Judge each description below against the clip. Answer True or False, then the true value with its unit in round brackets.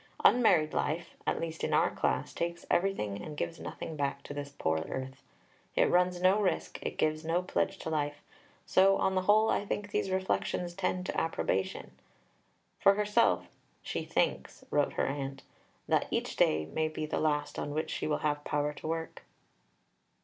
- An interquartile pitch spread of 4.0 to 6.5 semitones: True (4.3 semitones)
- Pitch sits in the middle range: True (160 Hz)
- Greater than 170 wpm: True (180 wpm)